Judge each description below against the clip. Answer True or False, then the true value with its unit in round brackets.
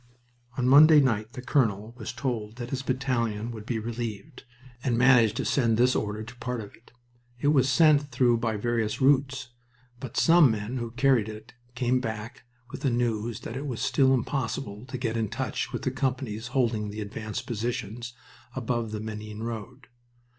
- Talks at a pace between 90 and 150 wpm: False (185 wpm)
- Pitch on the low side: True (120 Hz)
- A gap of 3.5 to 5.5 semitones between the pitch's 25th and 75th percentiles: False (2.9 semitones)